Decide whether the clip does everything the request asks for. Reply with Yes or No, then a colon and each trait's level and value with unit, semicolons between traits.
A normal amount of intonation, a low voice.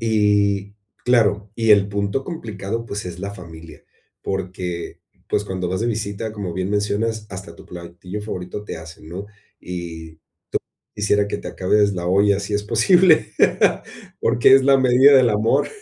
Yes: average, 3.2 semitones; low, 100 Hz